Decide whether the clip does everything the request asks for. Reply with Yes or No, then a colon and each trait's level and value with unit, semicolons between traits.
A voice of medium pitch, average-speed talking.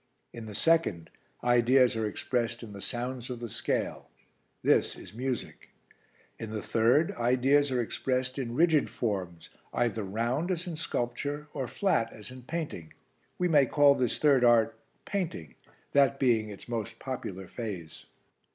No: low, 120 Hz; average, 150 wpm